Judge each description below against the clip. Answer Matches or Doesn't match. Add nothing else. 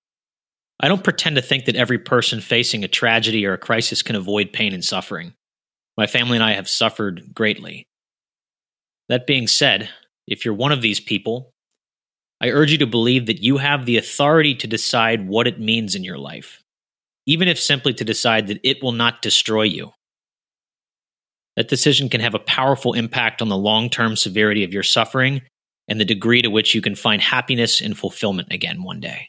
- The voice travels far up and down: Doesn't match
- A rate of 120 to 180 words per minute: Doesn't match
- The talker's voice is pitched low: Matches